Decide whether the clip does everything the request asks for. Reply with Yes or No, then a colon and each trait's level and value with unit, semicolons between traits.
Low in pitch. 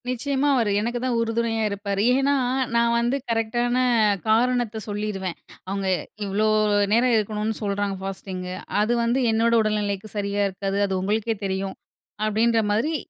No: high, 215 Hz